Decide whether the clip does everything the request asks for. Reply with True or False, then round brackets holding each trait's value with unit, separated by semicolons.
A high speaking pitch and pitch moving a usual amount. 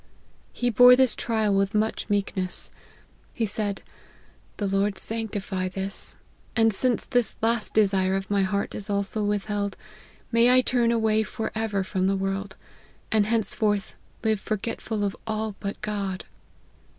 False (210 Hz; 2.2 semitones)